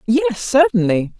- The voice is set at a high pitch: Yes, high, 195 Hz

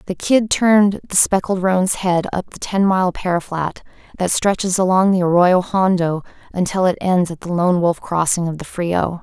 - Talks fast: No, average, 195 wpm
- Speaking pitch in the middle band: Yes, medium, 180 Hz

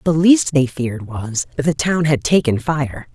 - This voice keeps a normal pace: No, fast, 210 wpm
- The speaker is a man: No, female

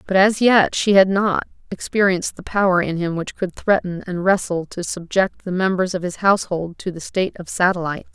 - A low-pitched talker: No, medium, 185 Hz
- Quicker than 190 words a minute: Yes, fast, 205 wpm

